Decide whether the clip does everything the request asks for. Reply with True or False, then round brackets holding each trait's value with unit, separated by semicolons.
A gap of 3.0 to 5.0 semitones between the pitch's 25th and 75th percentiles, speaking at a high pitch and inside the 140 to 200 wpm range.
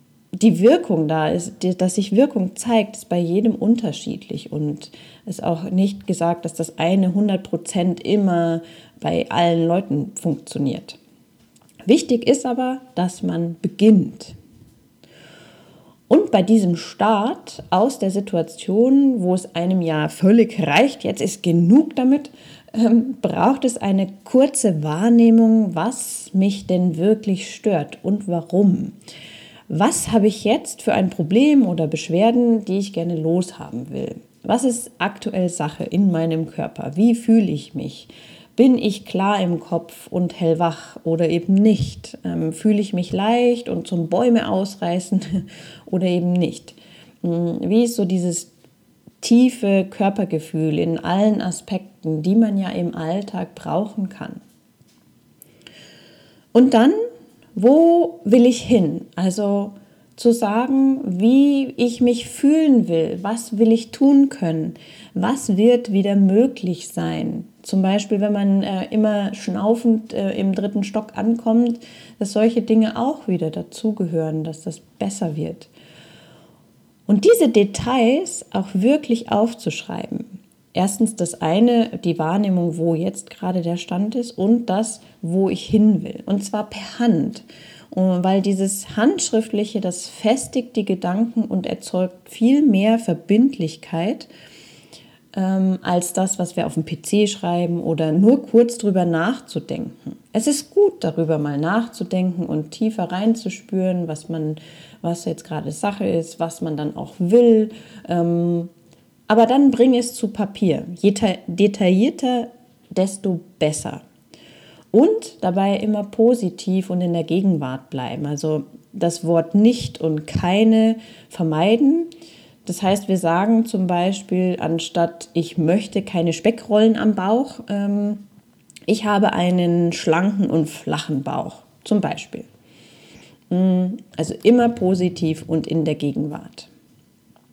False (4.7 semitones; 195 Hz; 130 wpm)